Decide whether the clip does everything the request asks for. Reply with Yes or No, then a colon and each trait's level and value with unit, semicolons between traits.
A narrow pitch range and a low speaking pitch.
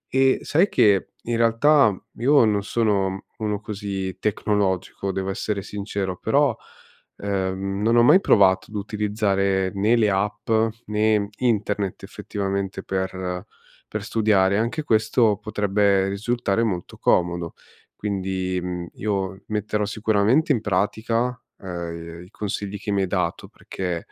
Yes: narrow, 2.2 semitones; low, 100 Hz